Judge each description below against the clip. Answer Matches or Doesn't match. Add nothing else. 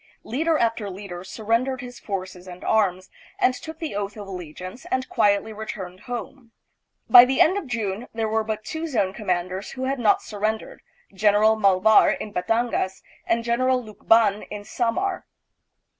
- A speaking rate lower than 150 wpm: Doesn't match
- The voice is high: Matches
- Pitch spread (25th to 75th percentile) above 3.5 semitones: Matches